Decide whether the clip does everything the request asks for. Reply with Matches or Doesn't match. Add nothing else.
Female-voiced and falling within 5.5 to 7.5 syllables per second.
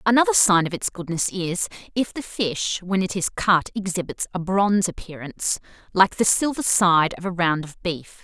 Doesn't match